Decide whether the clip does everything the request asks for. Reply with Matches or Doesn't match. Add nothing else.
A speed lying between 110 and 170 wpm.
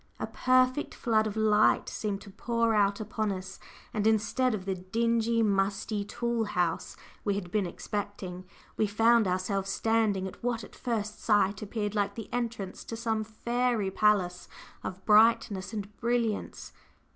Matches